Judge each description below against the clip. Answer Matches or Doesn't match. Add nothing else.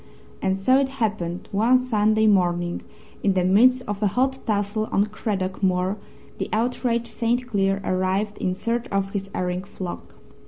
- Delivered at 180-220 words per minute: Doesn't match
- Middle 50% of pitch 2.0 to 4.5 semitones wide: Matches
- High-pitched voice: Matches